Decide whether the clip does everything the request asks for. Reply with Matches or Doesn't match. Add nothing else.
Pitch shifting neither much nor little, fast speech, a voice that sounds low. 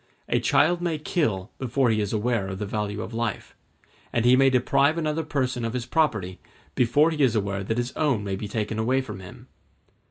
Matches